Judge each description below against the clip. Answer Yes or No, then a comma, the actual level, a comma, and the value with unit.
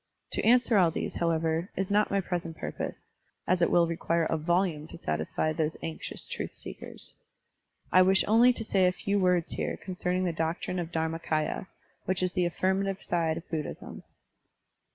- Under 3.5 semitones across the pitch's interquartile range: Yes, narrow, 2.6 semitones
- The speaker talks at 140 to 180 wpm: Yes, average, 175 wpm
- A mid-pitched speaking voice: Yes, medium, 175 Hz